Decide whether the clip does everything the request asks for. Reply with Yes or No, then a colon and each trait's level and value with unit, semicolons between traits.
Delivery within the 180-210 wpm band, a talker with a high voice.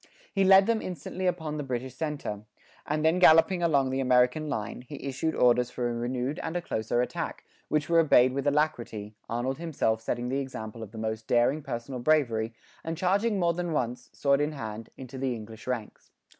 No: average, 195 wpm; low, 135 Hz